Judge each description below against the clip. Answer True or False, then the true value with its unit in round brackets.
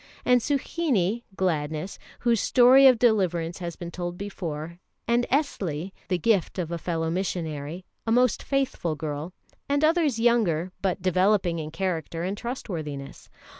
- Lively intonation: True (6.2 semitones)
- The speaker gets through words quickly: False (140 wpm)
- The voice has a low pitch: False (185 Hz)